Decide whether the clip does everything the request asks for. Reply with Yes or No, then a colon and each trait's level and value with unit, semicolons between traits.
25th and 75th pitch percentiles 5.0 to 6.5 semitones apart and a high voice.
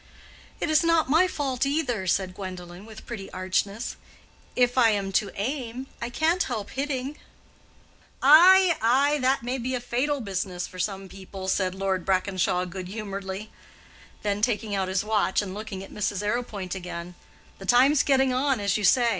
Yes: wide, 5.4 semitones; high, 215 Hz